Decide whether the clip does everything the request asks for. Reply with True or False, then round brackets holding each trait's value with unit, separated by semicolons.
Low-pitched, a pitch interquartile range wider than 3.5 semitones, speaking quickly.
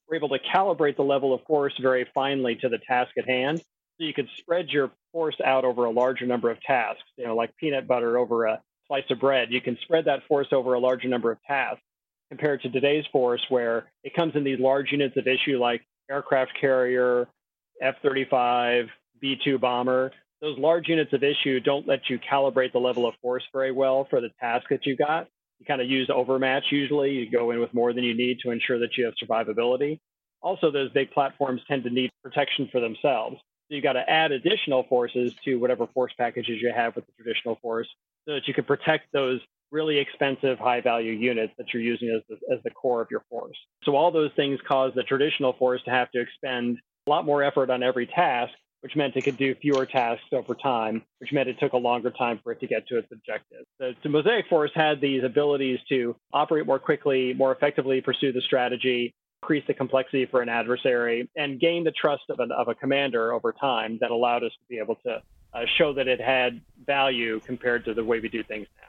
False (130 Hz; 2.4 semitones; 220 wpm)